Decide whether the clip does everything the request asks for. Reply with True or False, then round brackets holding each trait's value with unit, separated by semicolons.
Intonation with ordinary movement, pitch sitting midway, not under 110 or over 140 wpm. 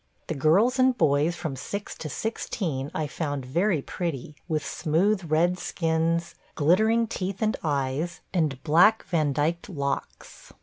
True (4.2 semitones; 165 Hz; 135 wpm)